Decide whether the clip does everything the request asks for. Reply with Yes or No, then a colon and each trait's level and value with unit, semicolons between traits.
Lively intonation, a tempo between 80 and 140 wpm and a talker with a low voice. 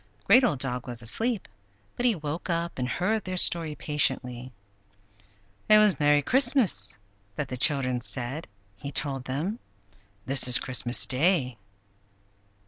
No: wide, 6.5 semitones; slow, 135 wpm; medium, 145 Hz